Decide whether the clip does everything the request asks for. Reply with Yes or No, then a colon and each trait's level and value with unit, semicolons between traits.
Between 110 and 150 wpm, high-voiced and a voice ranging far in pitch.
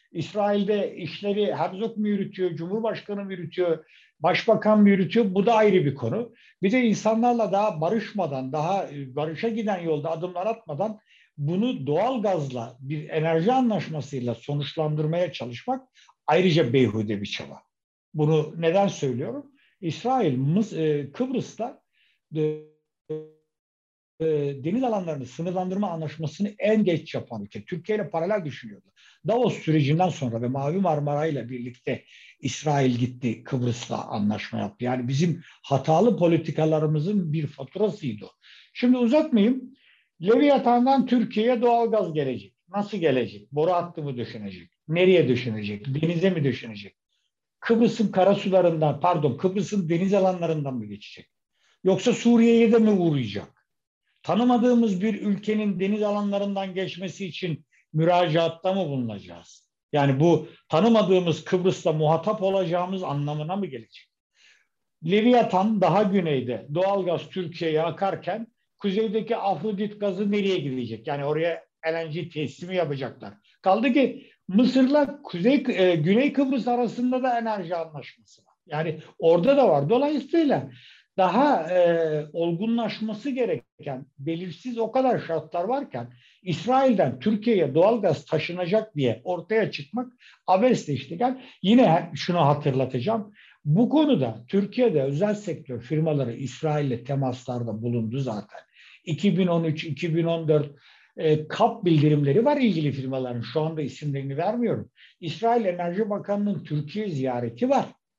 No: average, 115 wpm; medium, 175 Hz; wide, 6.5 semitones